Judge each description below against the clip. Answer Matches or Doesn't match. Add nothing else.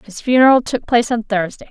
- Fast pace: Matches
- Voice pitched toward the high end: Matches